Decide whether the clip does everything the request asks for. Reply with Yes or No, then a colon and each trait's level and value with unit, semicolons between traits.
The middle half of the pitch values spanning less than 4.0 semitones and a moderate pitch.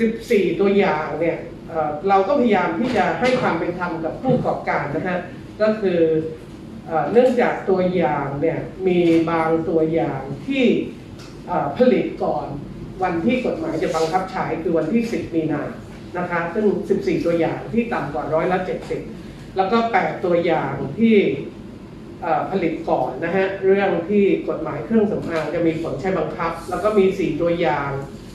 Yes: average, 3.3 semitones; medium, 170 Hz